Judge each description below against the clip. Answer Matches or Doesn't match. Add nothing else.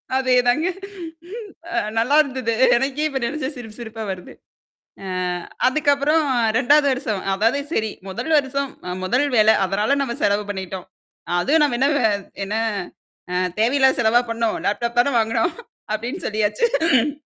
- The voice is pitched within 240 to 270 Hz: Matches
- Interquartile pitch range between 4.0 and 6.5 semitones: Matches